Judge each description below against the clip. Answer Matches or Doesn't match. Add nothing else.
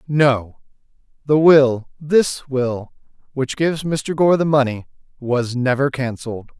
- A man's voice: Matches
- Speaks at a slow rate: Matches